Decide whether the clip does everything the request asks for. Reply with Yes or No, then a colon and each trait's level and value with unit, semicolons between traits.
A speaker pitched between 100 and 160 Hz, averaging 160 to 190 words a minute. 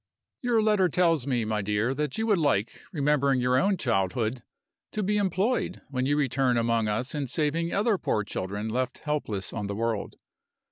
Yes: low, 135 Hz; average, 180 wpm